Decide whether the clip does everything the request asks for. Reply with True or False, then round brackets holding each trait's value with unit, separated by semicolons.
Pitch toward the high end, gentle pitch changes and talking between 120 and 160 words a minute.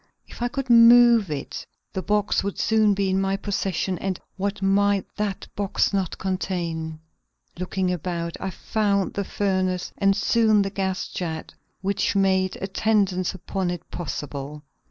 True (195 Hz; 1.9 semitones; 150 wpm)